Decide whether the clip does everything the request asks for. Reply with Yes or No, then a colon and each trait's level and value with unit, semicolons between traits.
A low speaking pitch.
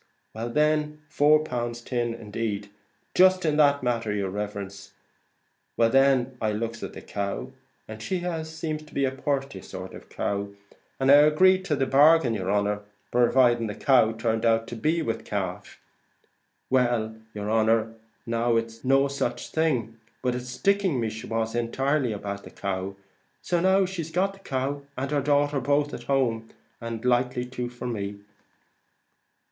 Yes: low, 120 Hz